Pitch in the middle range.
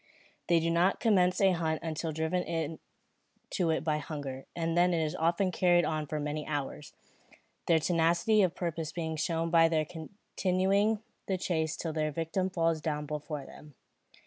Yes: medium, 165 Hz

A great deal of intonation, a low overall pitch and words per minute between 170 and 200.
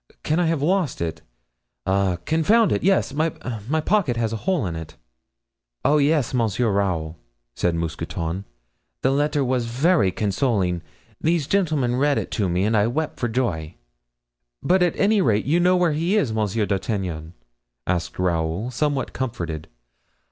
No: wide, 8.9 semitones; low, 120 Hz; average, 155 wpm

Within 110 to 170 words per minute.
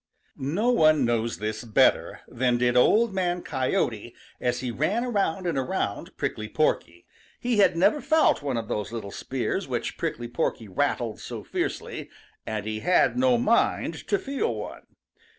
Yes: average, 160 wpm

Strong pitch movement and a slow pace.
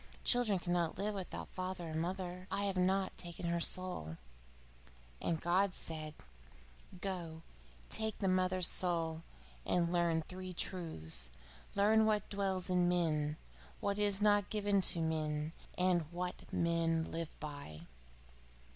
No: average, 2.8 semitones; slow, 130 wpm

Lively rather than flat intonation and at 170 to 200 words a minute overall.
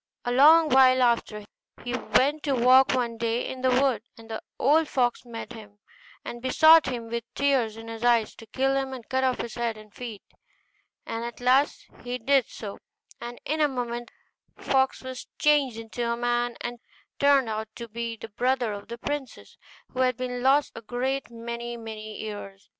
No: narrow, 2.5 semitones; average, 190 wpm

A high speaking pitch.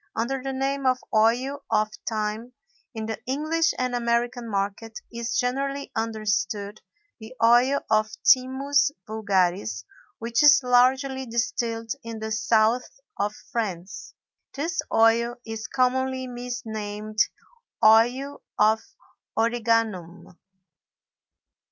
Yes: high, 235 Hz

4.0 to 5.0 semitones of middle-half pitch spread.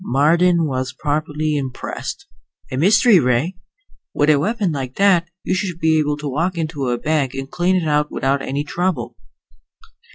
Yes: average, 4.3 semitones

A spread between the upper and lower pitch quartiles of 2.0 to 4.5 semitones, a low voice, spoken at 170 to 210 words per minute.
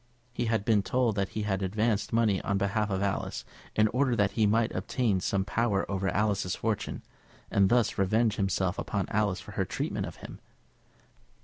Yes: narrow, 2.5 semitones; low, 105 Hz; average, 185 wpm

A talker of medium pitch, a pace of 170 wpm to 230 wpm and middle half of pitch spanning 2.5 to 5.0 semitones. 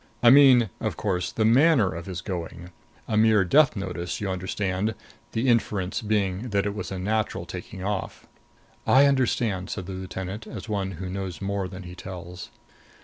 No: low, 100 Hz; average, 175 wpm; average, 3.1 semitones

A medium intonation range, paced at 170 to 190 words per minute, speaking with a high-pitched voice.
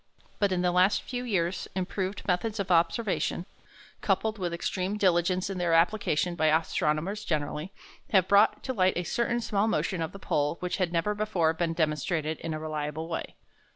No: average, 3.4 semitones; average, 180 wpm; medium, 180 Hz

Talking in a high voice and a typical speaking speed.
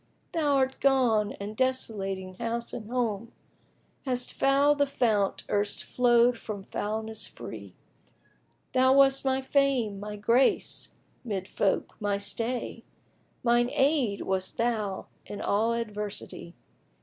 No: high, 230 Hz; slow, 125 wpm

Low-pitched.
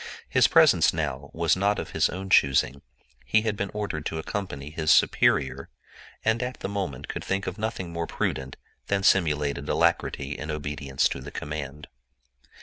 Yes: very low, 80 Hz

